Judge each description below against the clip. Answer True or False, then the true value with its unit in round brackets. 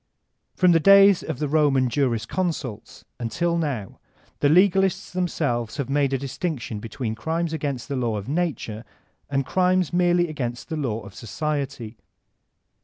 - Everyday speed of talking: True (145 wpm)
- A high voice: False (145 Hz)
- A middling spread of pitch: False (6.0 semitones)